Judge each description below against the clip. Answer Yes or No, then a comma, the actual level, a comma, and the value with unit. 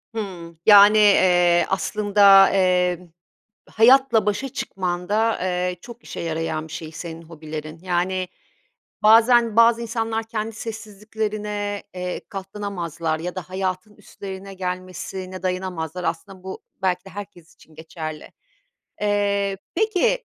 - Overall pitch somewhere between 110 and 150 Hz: No, high, 190 Hz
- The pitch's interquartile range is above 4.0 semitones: No, average, 3.0 semitones